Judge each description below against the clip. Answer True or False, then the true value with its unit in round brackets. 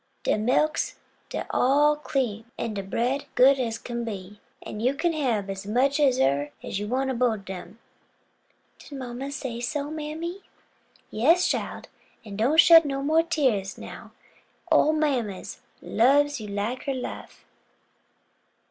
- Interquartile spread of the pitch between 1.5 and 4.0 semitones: False (5.1 semitones)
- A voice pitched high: True (255 Hz)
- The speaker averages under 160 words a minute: True (150 wpm)